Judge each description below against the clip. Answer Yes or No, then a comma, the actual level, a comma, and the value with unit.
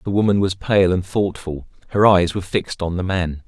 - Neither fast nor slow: No, fast, 225 wpm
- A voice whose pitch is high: No, very low, 95 Hz